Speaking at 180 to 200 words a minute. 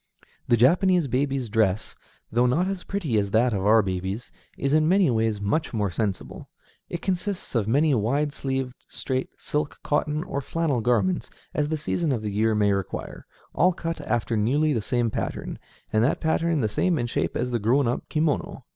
Yes: average, 190 wpm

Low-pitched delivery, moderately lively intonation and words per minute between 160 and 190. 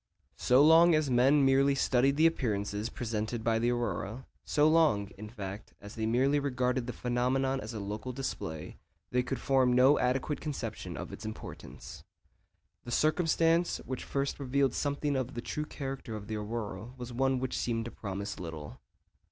Yes: low, 125 Hz; average, 3.9 semitones; average, 170 wpm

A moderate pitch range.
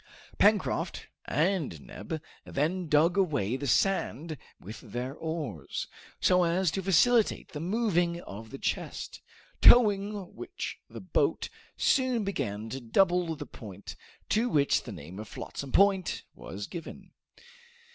No: wide, 7.0 semitones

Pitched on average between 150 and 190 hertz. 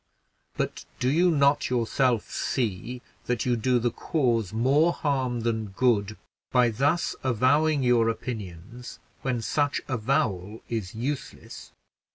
No: low, 125 Hz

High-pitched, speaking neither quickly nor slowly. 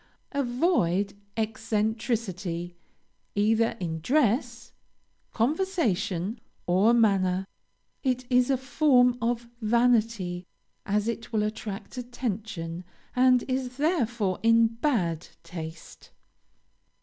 No: high, 225 Hz; slow, 90 wpm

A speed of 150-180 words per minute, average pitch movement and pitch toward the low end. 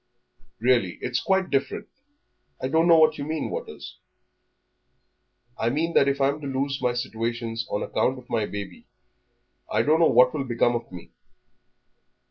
Yes: average, 165 wpm; average, 3.8 semitones; low, 130 Hz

